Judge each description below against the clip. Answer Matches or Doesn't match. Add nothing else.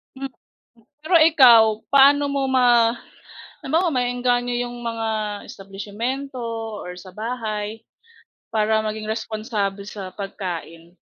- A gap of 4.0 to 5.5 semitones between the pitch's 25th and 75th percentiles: Doesn't match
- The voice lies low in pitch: Doesn't match